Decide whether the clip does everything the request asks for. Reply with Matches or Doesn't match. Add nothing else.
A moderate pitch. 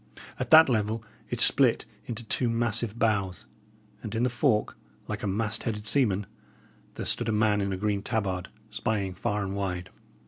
Doesn't match